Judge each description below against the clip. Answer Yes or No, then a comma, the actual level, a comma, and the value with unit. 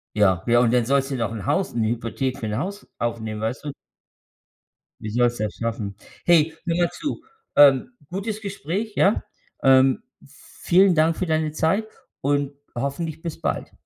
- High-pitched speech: No, medium, 140 Hz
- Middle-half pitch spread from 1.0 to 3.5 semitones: No, wide, 6.7 semitones